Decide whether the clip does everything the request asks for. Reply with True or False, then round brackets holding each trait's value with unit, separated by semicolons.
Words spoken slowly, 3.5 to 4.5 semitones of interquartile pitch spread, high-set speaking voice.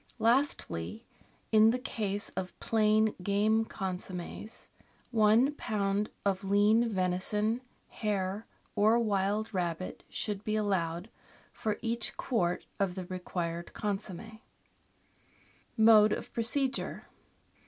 False (100 wpm; 2.8 semitones; 210 Hz)